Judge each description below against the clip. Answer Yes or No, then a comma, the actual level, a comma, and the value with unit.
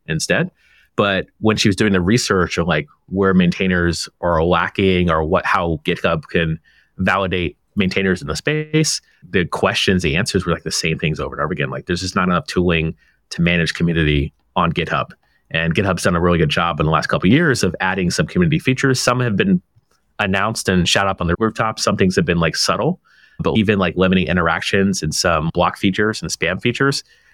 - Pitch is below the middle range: Yes, very low, 95 Hz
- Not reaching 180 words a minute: No, fast, 205 wpm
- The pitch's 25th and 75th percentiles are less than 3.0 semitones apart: No, average, 4.1 semitones